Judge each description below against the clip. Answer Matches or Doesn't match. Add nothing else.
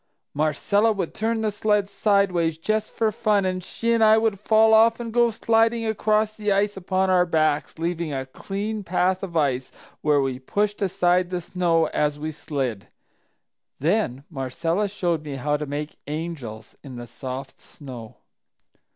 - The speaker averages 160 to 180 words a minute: Matches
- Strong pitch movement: Matches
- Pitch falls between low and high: Matches